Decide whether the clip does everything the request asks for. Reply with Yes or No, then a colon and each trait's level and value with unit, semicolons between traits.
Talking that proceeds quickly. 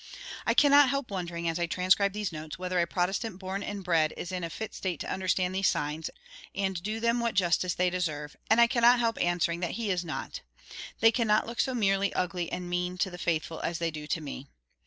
Yes: fast, 225 wpm